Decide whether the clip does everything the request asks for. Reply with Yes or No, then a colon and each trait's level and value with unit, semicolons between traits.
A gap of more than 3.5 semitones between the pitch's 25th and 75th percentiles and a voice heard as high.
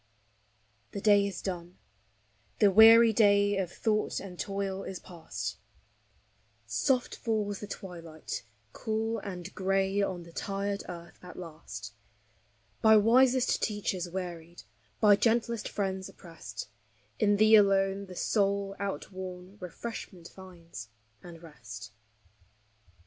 No: average, 2.9 semitones; high, 195 Hz